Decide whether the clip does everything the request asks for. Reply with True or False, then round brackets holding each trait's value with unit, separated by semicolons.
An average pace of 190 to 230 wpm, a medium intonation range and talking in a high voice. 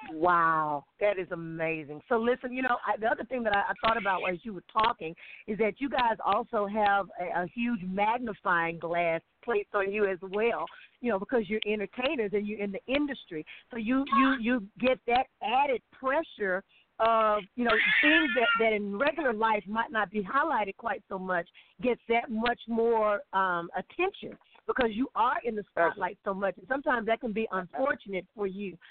True (195 wpm; 4.2 semitones; 215 Hz)